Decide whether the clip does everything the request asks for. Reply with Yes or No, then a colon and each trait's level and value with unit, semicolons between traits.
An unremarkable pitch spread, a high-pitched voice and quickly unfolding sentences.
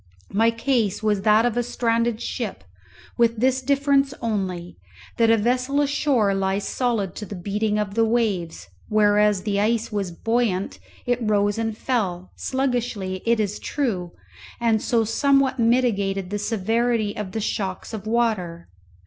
No: average, 3.0 semitones; high, 220 Hz; average, 150 wpm